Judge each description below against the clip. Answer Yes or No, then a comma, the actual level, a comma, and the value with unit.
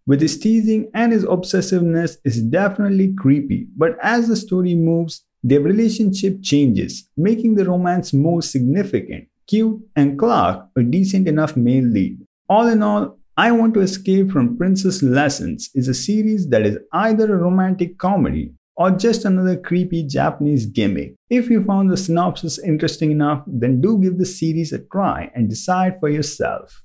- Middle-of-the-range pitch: Yes, medium, 180 Hz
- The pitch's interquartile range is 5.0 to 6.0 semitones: Yes, wide, 5.6 semitones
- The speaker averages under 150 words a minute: No, average, 165 wpm